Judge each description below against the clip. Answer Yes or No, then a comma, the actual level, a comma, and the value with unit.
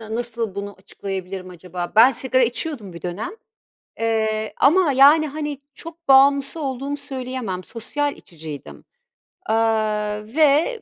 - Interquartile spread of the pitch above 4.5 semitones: Yes, average, 5.3 semitones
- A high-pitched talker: Yes, high, 235 Hz